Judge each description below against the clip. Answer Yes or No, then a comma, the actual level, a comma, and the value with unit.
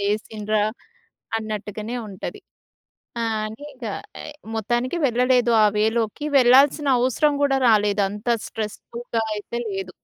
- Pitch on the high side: Yes, high, 225 Hz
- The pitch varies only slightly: No, average, 3.2 semitones